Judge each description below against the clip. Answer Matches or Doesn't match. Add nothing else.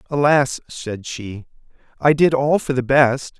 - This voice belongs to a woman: Doesn't match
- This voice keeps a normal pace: Matches